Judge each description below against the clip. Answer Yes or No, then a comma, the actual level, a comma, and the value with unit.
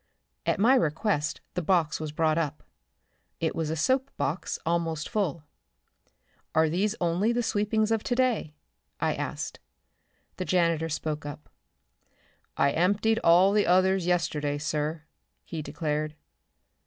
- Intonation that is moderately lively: Yes, average, 4.7 semitones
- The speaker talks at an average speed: No, slow, 130 wpm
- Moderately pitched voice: Yes, medium, 170 Hz